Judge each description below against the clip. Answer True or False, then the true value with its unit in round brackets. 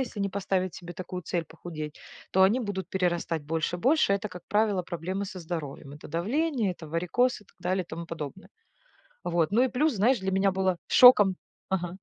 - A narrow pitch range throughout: False (3.3 semitones)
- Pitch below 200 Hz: True (185 Hz)